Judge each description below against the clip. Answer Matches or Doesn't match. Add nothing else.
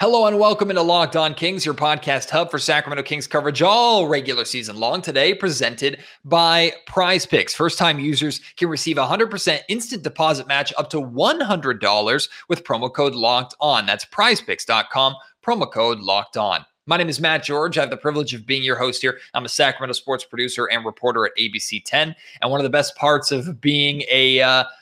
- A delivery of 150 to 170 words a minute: Doesn't match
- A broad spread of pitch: Doesn't match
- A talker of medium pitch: Matches